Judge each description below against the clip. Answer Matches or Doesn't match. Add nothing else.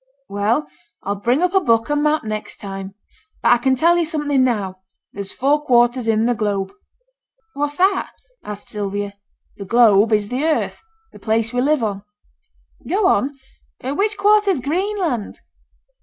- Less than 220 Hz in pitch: Doesn't match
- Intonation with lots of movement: Matches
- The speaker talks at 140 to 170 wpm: Matches